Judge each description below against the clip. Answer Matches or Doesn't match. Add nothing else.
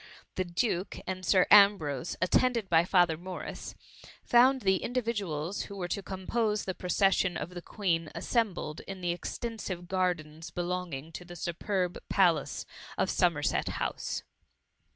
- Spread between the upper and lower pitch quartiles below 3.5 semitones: Matches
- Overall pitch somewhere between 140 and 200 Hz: Matches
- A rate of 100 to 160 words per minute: Matches